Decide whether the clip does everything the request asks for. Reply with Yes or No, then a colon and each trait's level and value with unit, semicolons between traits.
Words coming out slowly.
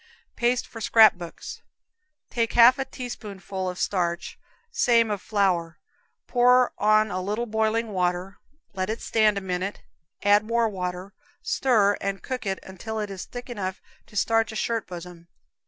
No: average, 155 wpm